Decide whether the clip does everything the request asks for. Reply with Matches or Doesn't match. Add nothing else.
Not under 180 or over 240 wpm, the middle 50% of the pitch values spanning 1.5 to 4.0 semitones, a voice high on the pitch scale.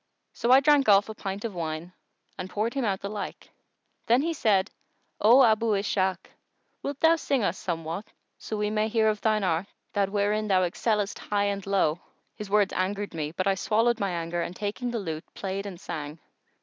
Matches